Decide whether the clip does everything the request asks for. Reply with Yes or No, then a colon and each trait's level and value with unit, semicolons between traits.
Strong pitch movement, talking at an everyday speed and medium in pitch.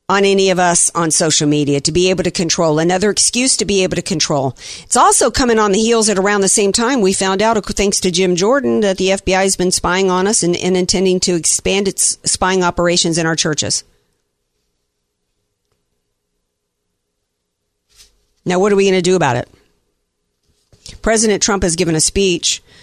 Yes: wide, 8.2 semitones; average, 185 wpm; medium, 180 Hz